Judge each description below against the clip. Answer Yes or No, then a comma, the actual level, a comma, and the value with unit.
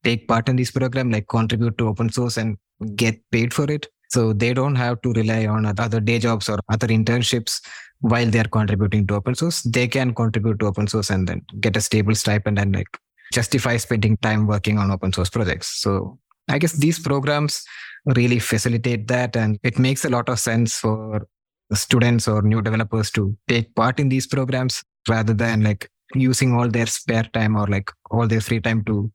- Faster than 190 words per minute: Yes, average, 200 wpm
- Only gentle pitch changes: Yes, narrow, 2.3 semitones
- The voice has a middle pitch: No, low, 115 Hz